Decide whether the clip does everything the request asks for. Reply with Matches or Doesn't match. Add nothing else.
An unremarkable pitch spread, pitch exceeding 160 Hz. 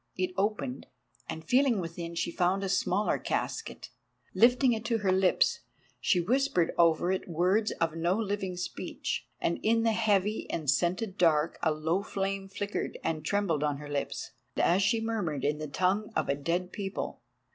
Matches